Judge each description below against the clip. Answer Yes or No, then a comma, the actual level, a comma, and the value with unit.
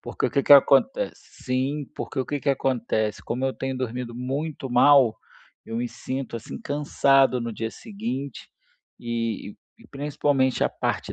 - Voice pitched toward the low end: Yes, low, 130 Hz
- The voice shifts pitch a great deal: No, average, 2.7 semitones